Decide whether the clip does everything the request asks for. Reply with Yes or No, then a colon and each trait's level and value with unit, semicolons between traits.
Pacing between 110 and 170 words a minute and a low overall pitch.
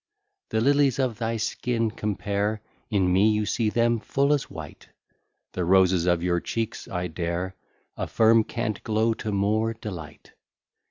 Yes: average, 150 wpm; low, 105 Hz